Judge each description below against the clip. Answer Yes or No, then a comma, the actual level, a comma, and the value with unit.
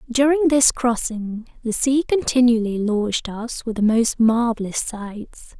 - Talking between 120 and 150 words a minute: Yes, average, 140 wpm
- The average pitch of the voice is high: Yes, high, 235 Hz